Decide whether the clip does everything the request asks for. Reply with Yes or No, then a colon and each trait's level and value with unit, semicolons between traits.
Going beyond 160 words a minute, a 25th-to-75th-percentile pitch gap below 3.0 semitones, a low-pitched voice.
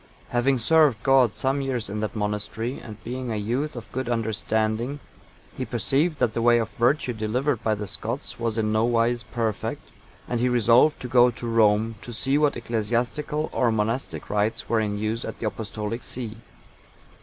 Yes: average, 185 wpm; narrow, 2.6 semitones; low, 115 Hz